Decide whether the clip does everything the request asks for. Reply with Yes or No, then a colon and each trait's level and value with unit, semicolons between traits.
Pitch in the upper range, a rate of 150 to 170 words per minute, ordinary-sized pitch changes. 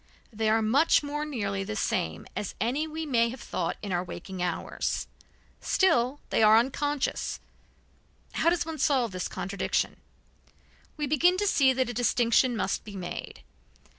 No: high, 240 Hz; average, 160 wpm; wide, 6.2 semitones